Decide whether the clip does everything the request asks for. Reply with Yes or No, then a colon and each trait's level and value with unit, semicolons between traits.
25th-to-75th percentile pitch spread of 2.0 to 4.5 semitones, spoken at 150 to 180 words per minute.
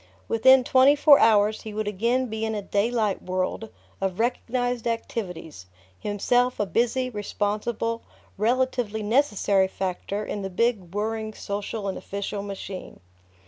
No: average, 3.0 semitones; slow, 135 wpm